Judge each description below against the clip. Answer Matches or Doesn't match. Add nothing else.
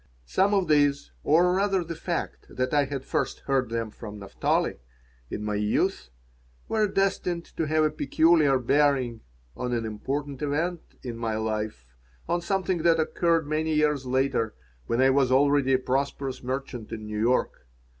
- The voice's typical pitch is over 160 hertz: Doesn't match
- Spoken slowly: Doesn't match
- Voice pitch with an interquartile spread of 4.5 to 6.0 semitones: Matches